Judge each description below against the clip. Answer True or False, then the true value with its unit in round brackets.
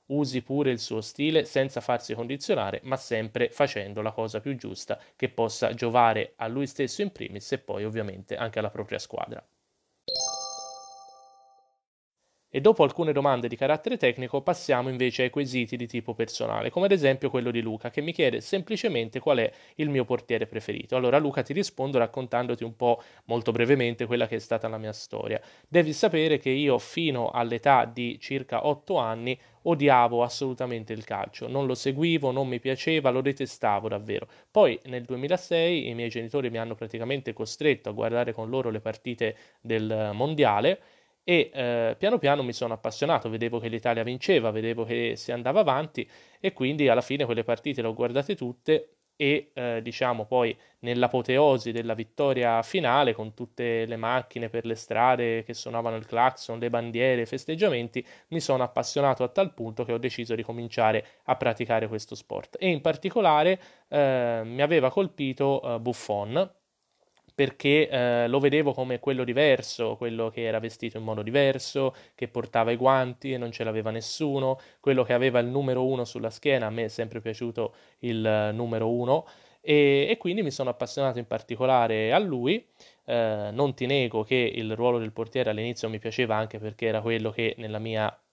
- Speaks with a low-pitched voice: True (125 Hz)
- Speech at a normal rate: False (175 wpm)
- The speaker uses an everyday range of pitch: True (3.1 semitones)